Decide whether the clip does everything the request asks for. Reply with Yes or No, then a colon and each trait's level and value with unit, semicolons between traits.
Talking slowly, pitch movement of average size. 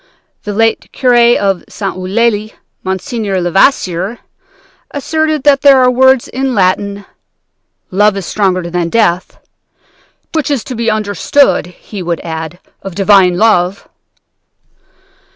Yes: slow, 130 wpm; average, 4.8 semitones